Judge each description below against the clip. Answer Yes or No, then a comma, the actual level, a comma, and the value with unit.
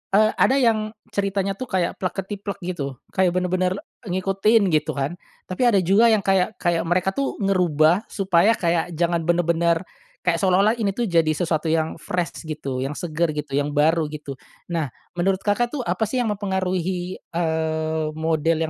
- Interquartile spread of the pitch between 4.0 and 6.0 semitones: No, average, 3.4 semitones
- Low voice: No, medium, 180 Hz